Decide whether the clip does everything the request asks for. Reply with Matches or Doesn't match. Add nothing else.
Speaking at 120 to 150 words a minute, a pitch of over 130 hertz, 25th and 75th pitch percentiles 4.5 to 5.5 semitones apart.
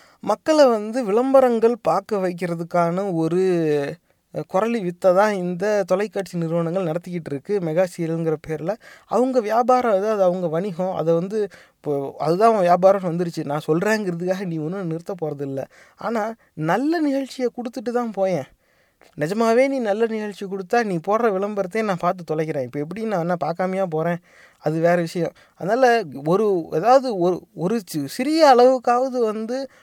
Matches